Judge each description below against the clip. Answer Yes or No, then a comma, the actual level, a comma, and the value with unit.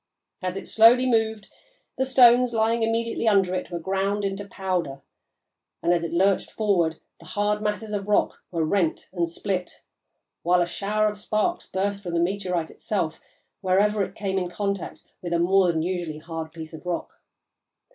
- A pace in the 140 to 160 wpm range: No, average, 175 wpm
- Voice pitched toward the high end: Yes, high, 195 Hz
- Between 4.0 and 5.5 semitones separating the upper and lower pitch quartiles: No, average, 3.3 semitones